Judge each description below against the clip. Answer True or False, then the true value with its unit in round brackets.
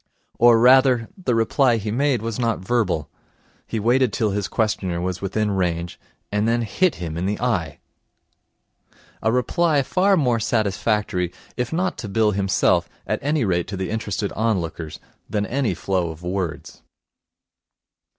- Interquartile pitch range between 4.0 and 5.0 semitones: True (4.6 semitones)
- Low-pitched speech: True (110 Hz)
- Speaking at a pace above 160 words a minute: False (150 wpm)